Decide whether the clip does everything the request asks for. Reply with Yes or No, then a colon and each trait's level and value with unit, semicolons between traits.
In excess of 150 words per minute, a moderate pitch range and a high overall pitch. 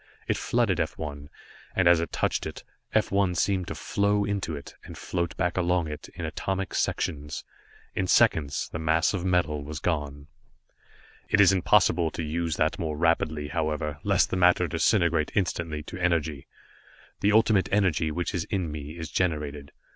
No: average, 170 wpm; average, 3.3 semitones; very low, 85 Hz